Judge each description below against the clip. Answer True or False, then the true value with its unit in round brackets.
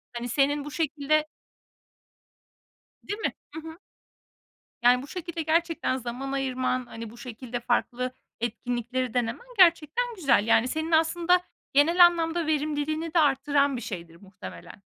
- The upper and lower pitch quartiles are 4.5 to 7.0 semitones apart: True (4.8 semitones)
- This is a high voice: True (285 Hz)